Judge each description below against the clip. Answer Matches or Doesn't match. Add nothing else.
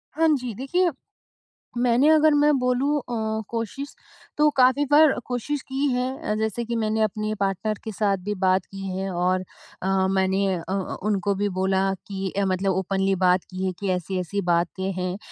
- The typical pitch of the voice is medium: Doesn't match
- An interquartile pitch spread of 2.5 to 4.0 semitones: Doesn't match